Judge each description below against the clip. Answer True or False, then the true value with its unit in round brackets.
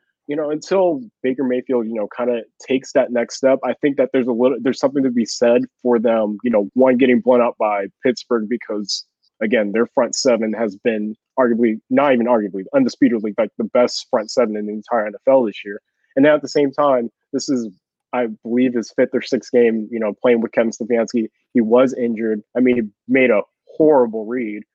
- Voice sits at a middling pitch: False (120 Hz)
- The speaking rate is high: True (215 wpm)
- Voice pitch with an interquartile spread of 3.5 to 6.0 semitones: False (2.7 semitones)